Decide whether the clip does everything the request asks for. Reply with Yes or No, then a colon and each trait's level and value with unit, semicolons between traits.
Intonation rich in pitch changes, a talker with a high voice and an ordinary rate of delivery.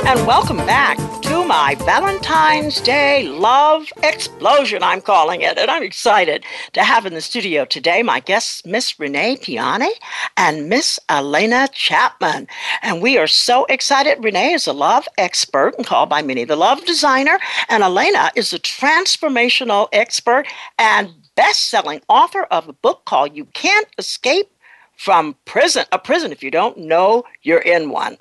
Yes: wide, 8.3 semitones; very high, 305 Hz; average, 160 wpm